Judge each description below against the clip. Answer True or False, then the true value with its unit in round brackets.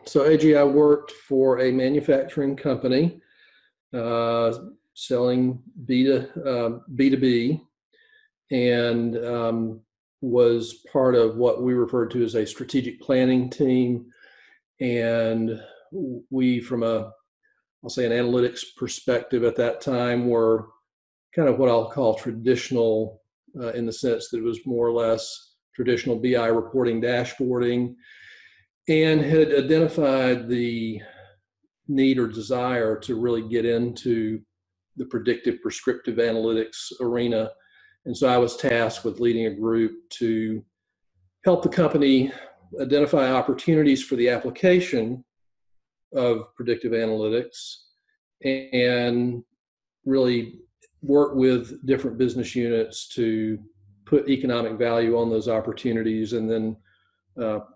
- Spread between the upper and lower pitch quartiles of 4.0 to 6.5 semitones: False (2.7 semitones)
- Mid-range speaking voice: False (120 Hz)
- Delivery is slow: True (120 wpm)